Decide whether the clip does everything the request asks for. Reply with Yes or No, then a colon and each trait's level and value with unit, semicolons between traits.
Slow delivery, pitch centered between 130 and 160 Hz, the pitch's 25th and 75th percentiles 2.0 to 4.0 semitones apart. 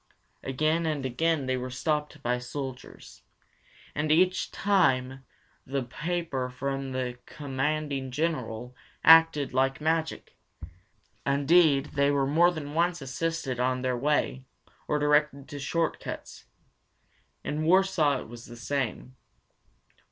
Yes: slow, 120 wpm; medium, 140 Hz; average, 3.5 semitones